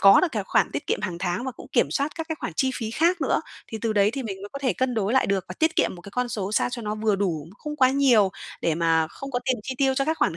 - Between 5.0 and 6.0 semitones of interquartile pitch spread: Yes, wide, 5.5 semitones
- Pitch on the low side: No, high, 230 Hz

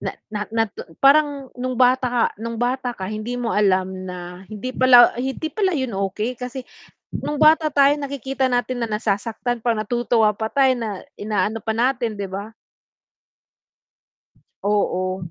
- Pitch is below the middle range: No, high, 235 Hz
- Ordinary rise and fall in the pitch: Yes, average, 3.6 semitones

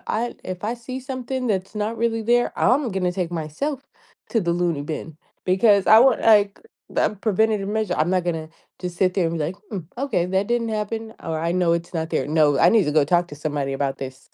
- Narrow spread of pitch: No, average, 5.3 semitones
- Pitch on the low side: No, medium, 185 Hz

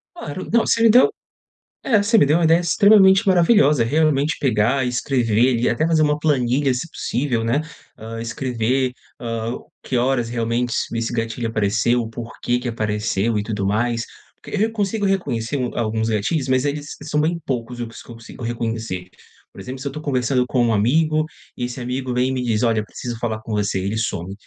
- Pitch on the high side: No, low, 125 Hz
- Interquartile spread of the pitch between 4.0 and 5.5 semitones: Yes, average, 4.5 semitones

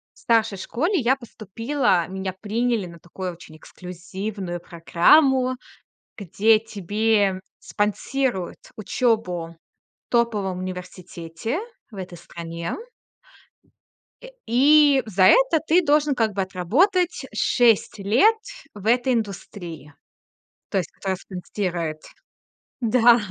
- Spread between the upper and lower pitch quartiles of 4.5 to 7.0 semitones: Yes, average, 5.2 semitones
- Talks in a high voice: Yes, high, 205 Hz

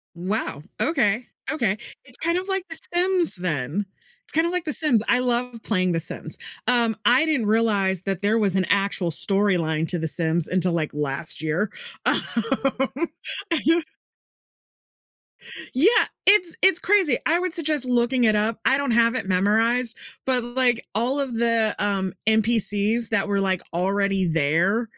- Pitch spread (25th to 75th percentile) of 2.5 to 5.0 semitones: No, wide, 5.4 semitones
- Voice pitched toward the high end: Yes, high, 220 Hz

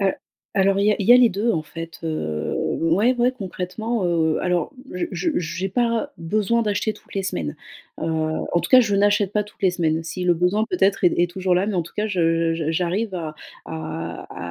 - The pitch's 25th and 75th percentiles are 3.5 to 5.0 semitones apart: Yes, average, 4.1 semitones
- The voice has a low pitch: No, medium, 185 Hz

